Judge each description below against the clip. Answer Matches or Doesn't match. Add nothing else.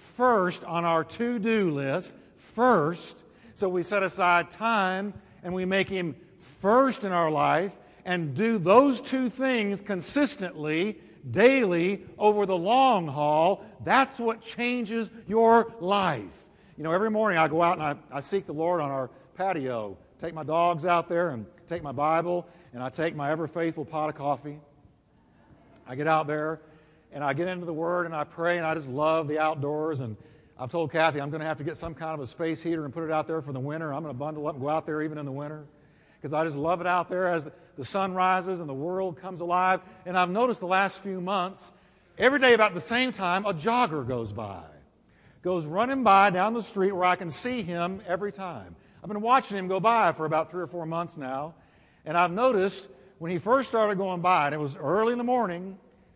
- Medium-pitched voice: Matches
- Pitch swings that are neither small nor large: Matches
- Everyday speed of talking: Doesn't match